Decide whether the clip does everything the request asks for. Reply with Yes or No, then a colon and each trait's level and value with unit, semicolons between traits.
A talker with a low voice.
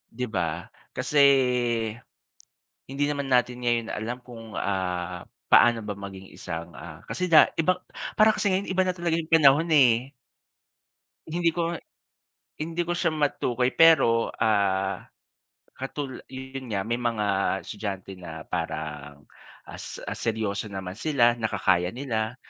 Yes: low, 120 Hz